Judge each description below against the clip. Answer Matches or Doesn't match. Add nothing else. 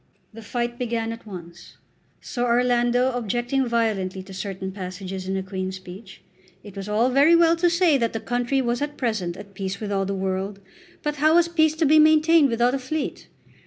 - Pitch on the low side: Doesn't match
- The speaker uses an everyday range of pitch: Doesn't match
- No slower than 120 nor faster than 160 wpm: Doesn't match